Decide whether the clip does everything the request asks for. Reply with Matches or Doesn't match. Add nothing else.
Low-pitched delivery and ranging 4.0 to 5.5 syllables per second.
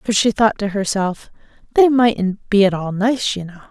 Doesn't match